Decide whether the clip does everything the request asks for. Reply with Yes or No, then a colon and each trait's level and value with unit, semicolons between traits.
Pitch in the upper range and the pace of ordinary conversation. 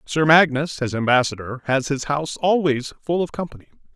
No: medium, 145 Hz; average, 165 wpm